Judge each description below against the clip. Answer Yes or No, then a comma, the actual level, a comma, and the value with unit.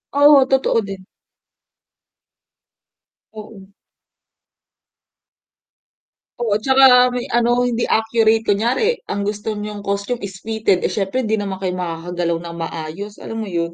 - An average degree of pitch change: Yes, average, 3.5 semitones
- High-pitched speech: Yes, high, 210 Hz